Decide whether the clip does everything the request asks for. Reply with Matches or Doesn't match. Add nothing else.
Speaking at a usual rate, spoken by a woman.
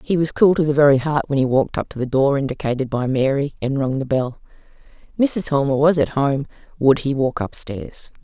Doesn't match